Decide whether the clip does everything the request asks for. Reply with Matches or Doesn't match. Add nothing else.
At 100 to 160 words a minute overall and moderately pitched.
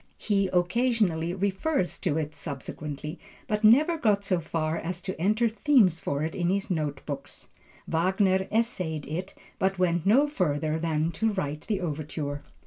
Matches